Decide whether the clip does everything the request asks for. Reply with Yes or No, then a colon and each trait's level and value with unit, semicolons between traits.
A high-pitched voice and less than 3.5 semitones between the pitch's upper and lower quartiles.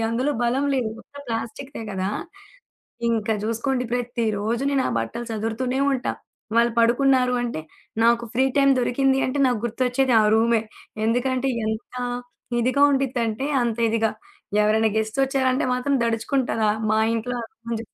Yes: high, 240 Hz; average, 2.7 semitones